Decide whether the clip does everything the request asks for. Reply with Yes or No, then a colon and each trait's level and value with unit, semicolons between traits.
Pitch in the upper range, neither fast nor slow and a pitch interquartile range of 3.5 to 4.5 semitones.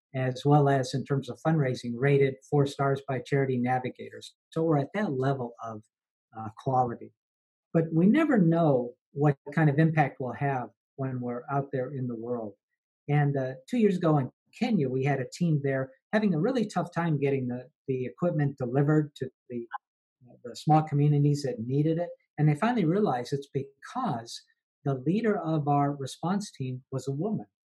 No: medium, 140 Hz; average, 180 wpm; average, 3.8 semitones